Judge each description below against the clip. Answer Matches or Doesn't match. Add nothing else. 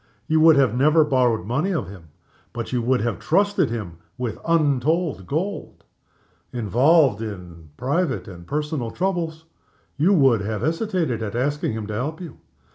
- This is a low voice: Matches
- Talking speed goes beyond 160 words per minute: Doesn't match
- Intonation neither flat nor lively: Doesn't match